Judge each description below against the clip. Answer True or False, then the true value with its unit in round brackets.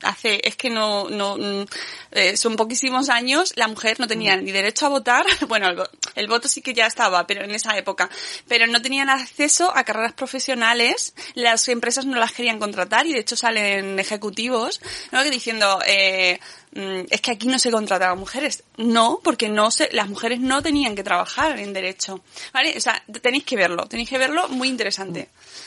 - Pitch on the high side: True (230 Hz)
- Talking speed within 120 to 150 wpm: False (185 wpm)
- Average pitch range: True (4.5 semitones)